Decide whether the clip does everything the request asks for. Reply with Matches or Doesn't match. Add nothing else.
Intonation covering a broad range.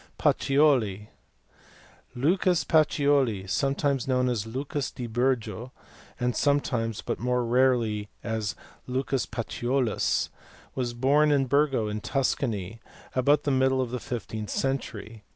Doesn't match